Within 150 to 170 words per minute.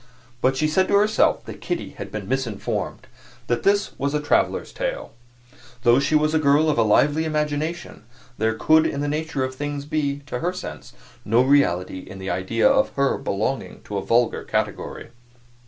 No: average, 185 wpm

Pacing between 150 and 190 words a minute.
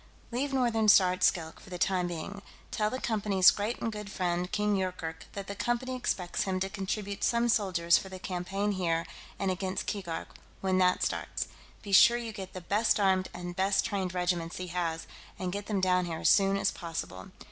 No: average, 200 wpm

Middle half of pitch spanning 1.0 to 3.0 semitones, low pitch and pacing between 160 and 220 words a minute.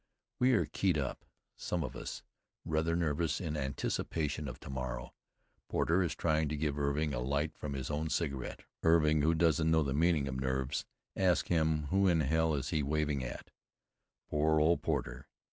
Yes: narrow, 2.5 semitones; very low, 75 Hz; average, 180 wpm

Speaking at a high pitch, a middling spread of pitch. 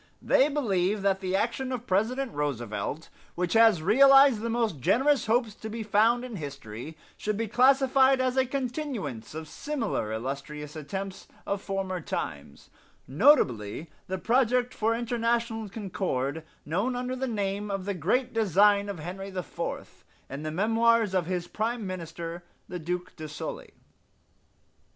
No: high, 200 Hz; wide, 6.1 semitones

